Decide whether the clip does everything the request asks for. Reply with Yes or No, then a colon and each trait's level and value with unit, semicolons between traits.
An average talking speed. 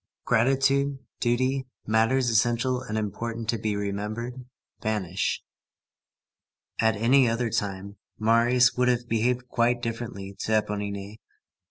No: slow, 115 wpm